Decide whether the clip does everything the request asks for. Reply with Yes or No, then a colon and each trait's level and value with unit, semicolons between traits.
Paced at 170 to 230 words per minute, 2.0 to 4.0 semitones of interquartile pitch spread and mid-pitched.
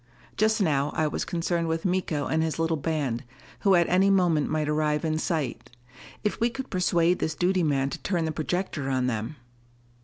Yes: average, 190 wpm; average, 3.2 semitones; medium, 160 Hz